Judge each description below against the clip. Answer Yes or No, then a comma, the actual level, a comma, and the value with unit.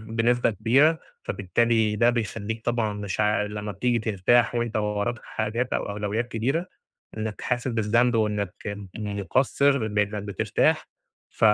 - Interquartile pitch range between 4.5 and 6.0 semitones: No, narrow, 2.5 semitones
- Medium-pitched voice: No, low, 110 Hz